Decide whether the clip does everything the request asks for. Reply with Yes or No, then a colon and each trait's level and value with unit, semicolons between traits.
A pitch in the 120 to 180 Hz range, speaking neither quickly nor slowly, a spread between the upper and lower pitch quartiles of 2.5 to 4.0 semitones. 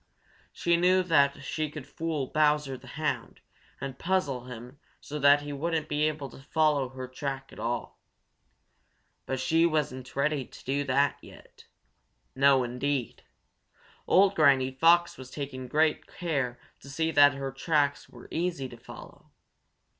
Yes: medium, 140 Hz; average, 150 wpm; average, 2.9 semitones